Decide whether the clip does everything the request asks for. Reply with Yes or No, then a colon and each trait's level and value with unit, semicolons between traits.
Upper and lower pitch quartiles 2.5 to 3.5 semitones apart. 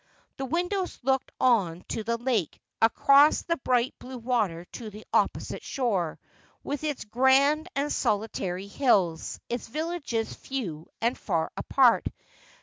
No: average, 4.9 semitones